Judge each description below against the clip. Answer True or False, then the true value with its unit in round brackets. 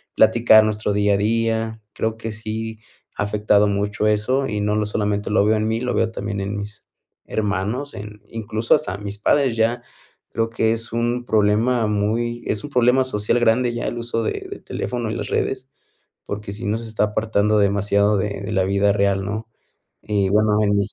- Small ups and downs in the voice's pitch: True (1.9 semitones)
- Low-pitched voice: True (110 Hz)